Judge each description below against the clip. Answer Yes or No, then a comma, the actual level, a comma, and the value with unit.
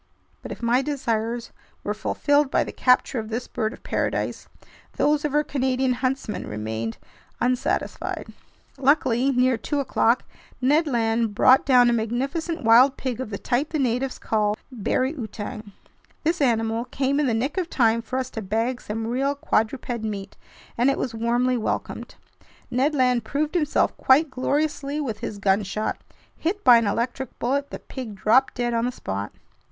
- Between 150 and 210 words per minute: Yes, average, 170 wpm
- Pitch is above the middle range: Yes, very high, 250 Hz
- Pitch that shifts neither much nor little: Yes, average, 3.4 semitones